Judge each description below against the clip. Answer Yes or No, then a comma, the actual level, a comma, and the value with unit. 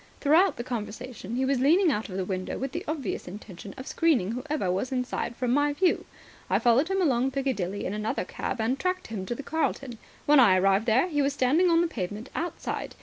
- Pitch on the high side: Yes, very high, 255 Hz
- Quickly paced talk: Yes, fast, 215 wpm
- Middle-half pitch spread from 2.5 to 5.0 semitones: No, wide, 5.5 semitones